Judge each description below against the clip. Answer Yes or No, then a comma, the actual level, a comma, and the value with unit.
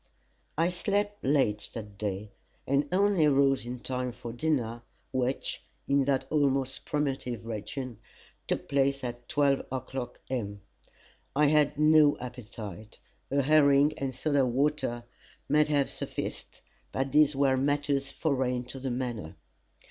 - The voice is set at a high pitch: No, low, 135 Hz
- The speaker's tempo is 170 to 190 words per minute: No, slow, 135 wpm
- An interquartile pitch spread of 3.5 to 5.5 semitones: No, average, 3.1 semitones